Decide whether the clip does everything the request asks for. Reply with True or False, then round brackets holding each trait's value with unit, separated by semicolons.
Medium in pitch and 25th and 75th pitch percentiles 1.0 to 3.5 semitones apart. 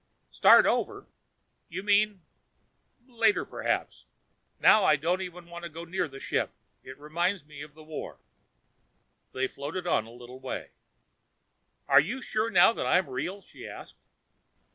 False (170 Hz; 5.0 semitones)